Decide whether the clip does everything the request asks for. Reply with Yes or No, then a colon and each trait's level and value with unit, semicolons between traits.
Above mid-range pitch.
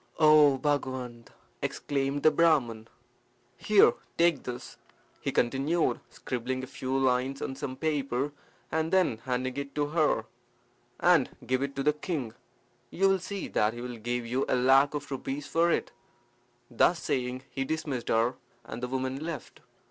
No: low, 135 Hz